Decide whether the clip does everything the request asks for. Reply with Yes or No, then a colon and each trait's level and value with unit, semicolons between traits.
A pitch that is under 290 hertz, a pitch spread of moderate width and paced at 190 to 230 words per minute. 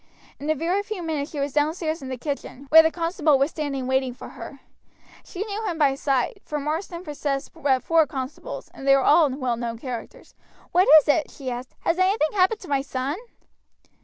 No: very high, 295 Hz; average, 3.6 semitones; fast, 205 wpm